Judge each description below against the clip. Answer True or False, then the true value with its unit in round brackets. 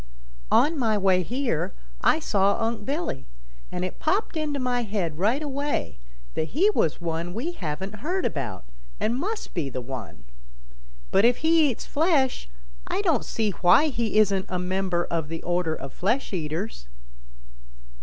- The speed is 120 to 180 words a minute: True (160 wpm)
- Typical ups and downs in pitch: False (8.4 semitones)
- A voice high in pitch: True (205 Hz)